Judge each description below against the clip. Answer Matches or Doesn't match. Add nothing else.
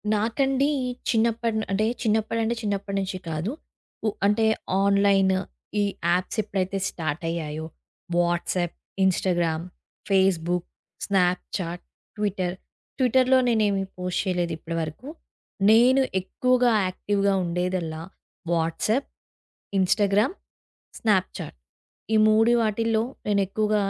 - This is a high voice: Matches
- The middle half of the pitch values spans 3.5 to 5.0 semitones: Matches